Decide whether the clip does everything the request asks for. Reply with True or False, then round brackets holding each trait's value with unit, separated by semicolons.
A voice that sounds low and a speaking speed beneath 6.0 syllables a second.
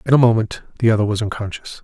False (110 Hz; 7.0 syllables/s)